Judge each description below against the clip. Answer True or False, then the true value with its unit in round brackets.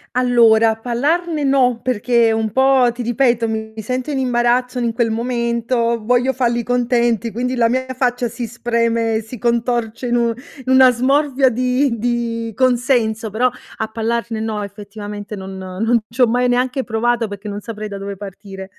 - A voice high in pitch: True (235 Hz)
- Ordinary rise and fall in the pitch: False (2.1 semitones)